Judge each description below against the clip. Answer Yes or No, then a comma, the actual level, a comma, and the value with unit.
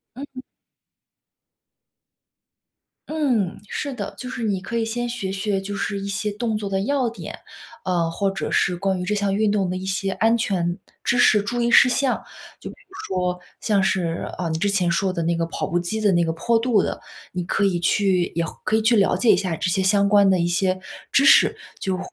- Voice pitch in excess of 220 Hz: No, high, 195 Hz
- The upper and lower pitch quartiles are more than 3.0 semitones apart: Yes, average, 3.5 semitones